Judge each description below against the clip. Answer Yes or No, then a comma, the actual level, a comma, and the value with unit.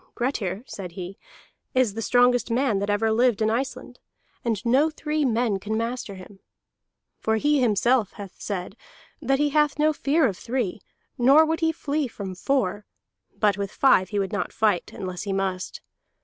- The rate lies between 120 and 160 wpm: No, average, 175 wpm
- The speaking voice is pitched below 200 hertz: No, high, 225 Hz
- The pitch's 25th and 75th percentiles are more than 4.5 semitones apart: Yes, average, 5.2 semitones